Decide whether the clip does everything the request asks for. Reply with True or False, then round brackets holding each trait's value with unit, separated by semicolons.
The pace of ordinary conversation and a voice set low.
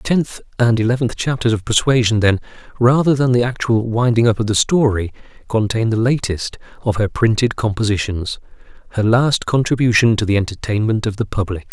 True (170 wpm; 115 Hz)